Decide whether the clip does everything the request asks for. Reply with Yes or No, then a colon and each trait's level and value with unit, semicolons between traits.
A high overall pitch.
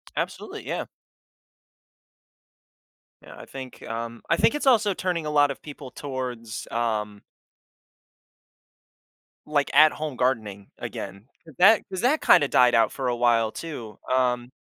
No: low, 130 Hz